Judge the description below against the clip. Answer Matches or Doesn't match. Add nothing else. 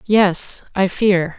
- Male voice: Doesn't match